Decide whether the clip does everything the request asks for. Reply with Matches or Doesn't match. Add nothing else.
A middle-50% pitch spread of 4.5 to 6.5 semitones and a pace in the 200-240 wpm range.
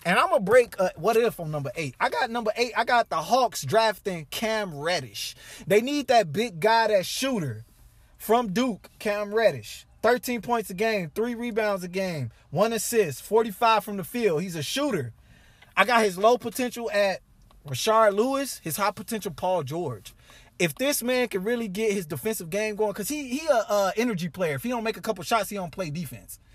Matches